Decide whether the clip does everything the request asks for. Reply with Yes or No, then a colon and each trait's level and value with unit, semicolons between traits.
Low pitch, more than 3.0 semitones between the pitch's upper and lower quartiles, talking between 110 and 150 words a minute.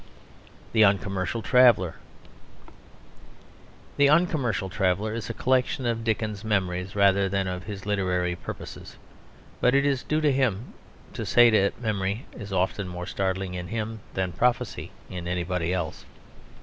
Yes: low, 100 Hz; average, 4.0 semitones; average, 140 wpm